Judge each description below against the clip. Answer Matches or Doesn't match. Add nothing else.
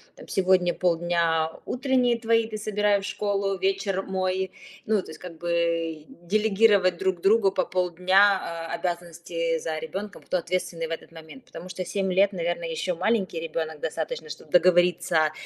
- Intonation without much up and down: Doesn't match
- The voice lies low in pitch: Doesn't match